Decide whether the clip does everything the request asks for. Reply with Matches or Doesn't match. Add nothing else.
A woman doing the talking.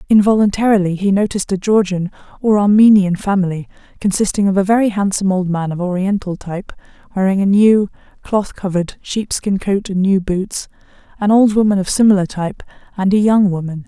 Matches